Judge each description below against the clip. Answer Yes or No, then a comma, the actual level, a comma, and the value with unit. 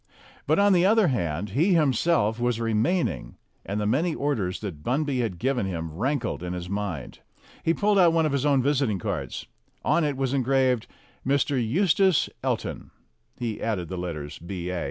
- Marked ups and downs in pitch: Yes, wide, 7.5 semitones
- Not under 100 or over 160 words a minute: No, average, 175 wpm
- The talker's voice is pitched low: Yes, low, 120 Hz